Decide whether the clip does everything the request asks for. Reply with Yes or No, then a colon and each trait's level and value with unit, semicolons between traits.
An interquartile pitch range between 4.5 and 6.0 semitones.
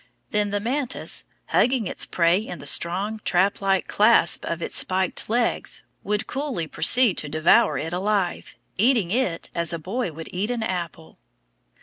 Yes: average, 5.0 semitones